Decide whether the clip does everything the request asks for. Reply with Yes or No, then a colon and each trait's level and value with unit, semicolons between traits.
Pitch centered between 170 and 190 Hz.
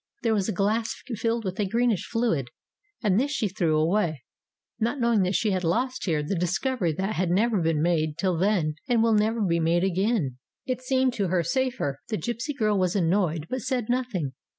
No: high, 200 Hz